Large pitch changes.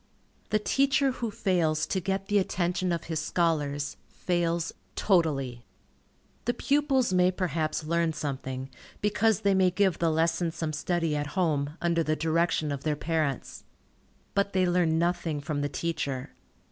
No: average, 3.4 semitones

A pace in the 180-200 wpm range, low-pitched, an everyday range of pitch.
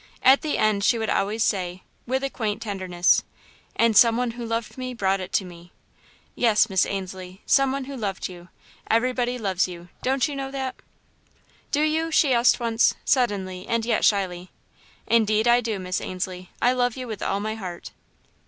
No: average, 185 wpm; high, 220 Hz; average, 4.8 semitones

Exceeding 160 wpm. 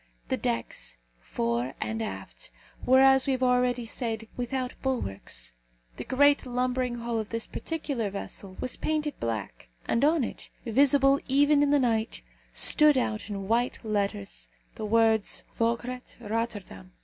No: average, 145 wpm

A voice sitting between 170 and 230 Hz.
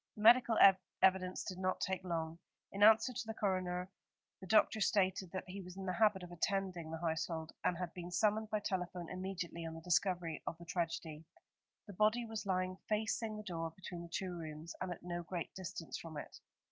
Yes: medium, 185 Hz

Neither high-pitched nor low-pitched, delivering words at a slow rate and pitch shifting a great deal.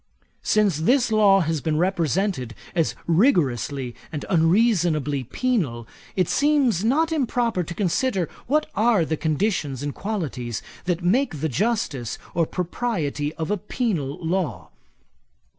Yes: medium, 175 Hz; slow, 125 wpm; wide, 6.6 semitones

